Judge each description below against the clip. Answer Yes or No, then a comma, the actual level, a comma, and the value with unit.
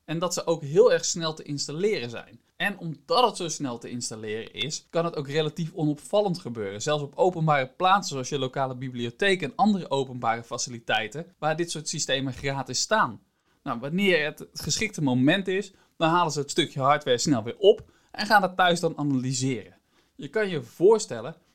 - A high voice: No, medium, 155 Hz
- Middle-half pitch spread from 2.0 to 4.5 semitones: No, wide, 5.5 semitones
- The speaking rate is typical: Yes, average, 185 wpm